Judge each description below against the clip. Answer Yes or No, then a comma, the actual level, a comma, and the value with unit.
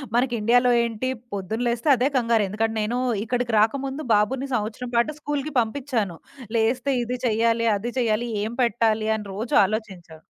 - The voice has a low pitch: No, high, 230 Hz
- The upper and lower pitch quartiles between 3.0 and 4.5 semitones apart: No, narrow, 2.5 semitones